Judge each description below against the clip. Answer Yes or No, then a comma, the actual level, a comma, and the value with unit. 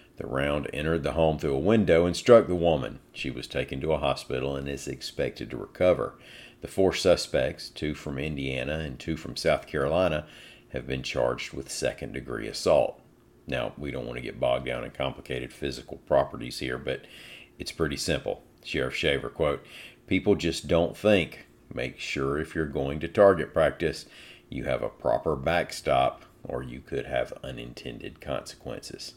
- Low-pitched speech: Yes, very low, 80 Hz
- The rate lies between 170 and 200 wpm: Yes, average, 175 wpm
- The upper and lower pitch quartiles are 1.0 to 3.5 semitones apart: No, average, 4.0 semitones